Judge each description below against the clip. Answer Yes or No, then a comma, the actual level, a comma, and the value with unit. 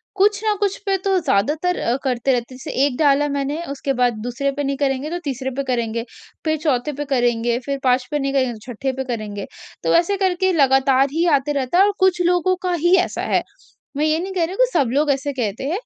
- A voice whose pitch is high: Yes, very high, 280 Hz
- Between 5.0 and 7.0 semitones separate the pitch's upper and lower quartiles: Yes, average, 5.3 semitones